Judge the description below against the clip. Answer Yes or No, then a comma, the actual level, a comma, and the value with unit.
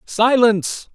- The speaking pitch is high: Yes, high, 230 Hz